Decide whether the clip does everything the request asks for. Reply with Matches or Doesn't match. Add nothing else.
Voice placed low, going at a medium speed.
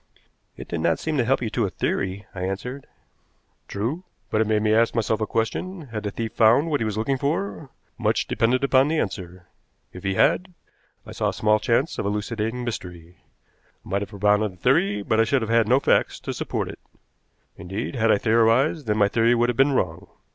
Doesn't match